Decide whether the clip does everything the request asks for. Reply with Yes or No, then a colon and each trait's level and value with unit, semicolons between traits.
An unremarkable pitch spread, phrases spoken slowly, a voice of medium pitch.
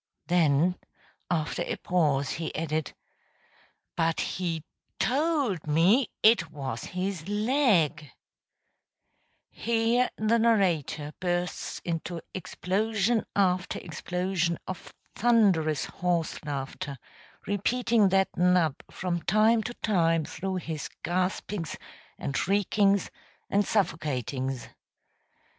Yes: average, 4.4 semitones; slow, 95 wpm; medium, 180 Hz